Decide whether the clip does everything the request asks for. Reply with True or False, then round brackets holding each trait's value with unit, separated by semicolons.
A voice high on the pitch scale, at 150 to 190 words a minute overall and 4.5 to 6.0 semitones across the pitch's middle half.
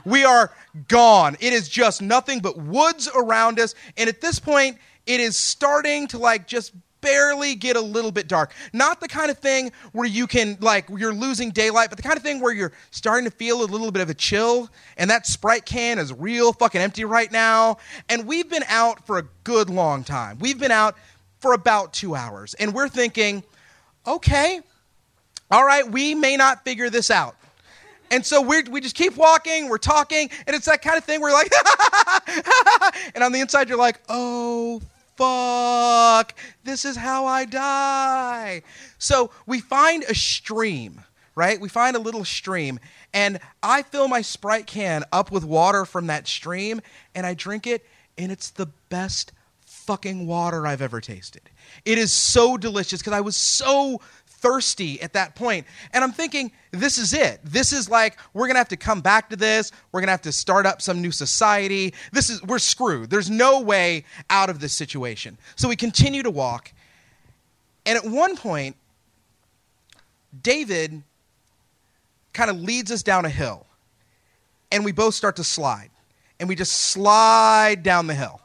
True (225 Hz; 185 wpm; 5.6 semitones)